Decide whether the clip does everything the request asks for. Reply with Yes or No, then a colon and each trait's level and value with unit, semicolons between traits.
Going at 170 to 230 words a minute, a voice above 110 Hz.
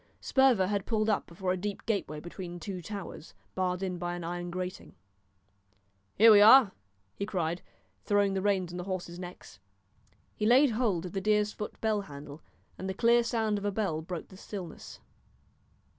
Yes: average, 180 wpm; high, 190 Hz